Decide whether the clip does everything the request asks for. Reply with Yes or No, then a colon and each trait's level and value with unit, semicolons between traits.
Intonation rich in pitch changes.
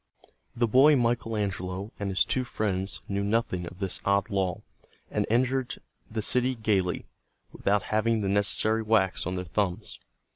No: average, 3.1 semitones